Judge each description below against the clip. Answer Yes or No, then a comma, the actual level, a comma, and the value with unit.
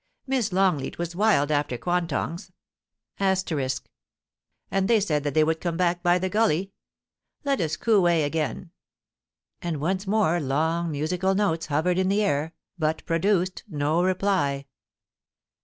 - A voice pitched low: No, medium, 175 Hz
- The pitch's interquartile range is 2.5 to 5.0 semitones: Yes, average, 3.7 semitones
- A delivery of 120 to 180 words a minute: Yes, average, 140 wpm